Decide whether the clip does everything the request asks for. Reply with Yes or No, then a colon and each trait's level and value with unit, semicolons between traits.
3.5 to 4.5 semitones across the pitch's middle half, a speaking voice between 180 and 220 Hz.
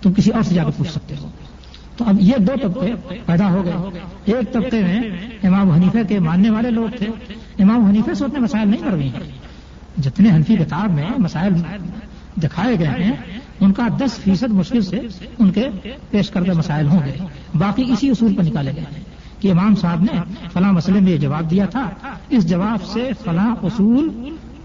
Yes: average, 3.9 semitones; high, 195 Hz